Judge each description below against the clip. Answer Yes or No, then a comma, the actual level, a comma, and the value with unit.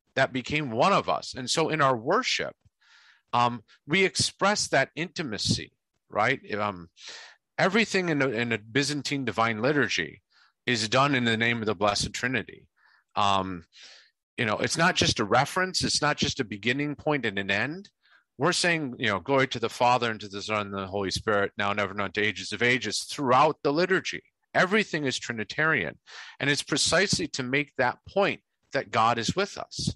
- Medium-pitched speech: No, low, 130 Hz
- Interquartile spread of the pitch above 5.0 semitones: Yes, wide, 5.6 semitones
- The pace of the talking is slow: No, average, 185 wpm